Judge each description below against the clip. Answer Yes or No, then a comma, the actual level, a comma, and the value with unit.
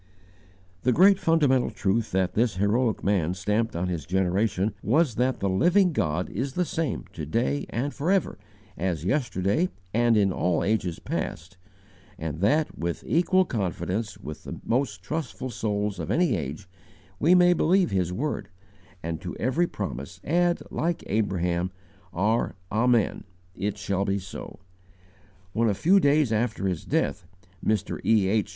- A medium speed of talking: Yes, average, 150 wpm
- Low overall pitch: Yes, low, 105 Hz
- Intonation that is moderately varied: No, wide, 7.3 semitones